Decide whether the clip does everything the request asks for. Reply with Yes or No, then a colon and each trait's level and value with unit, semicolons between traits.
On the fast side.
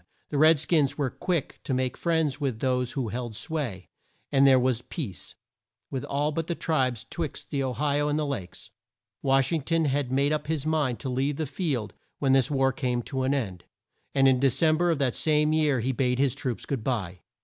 Yes: fast, 215 wpm